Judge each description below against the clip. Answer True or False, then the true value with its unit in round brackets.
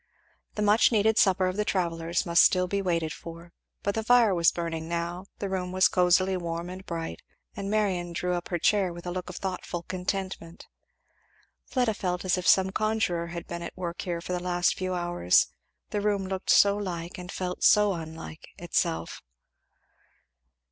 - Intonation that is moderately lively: False (2.2 semitones)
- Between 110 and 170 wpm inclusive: False (180 wpm)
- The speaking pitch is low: False (180 Hz)